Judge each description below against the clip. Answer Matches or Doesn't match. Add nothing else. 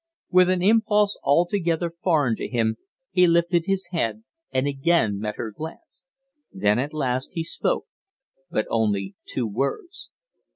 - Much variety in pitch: Matches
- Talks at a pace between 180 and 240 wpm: Doesn't match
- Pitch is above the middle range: Doesn't match